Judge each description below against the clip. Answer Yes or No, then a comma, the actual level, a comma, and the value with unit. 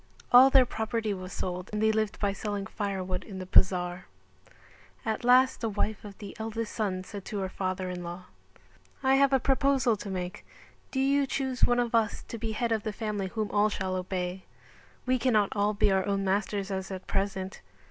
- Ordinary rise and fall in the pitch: Yes, average, 3.3 semitones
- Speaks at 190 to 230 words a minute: Yes, average, 200 wpm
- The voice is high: Yes, high, 205 Hz